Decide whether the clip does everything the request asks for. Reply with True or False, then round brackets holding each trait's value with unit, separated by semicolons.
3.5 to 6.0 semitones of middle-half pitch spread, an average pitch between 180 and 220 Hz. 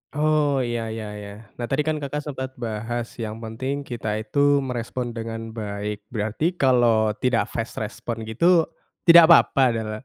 False (4.1 semitones; 120 Hz)